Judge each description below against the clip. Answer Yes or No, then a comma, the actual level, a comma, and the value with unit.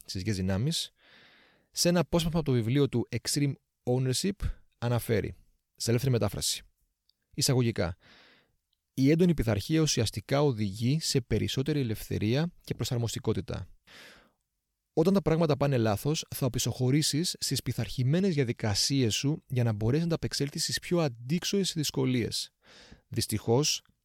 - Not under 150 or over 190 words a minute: No, average, 120 wpm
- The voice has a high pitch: No, low, 125 Hz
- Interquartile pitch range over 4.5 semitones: Yes, average, 5.0 semitones